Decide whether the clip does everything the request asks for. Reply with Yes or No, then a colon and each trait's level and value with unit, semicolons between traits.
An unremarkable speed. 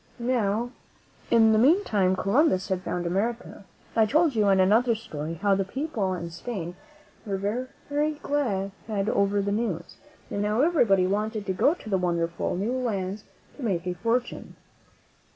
Yes: average, 160 wpm